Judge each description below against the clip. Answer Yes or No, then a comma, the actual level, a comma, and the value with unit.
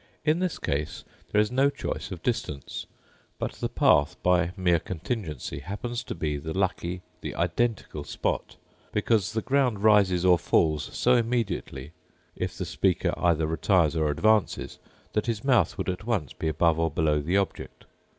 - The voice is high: No, very low, 90 Hz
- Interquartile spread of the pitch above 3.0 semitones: Yes, wide, 5.6 semitones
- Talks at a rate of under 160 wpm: No, average, 165 wpm